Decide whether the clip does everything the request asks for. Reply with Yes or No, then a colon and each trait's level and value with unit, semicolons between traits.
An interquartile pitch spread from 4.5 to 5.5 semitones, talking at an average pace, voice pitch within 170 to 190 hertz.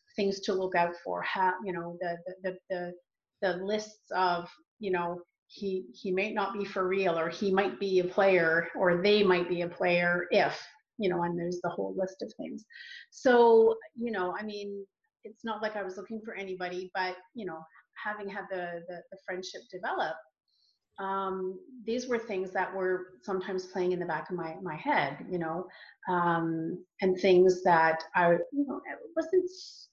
No: average, 2.7 semitones; average, 190 wpm; medium, 185 Hz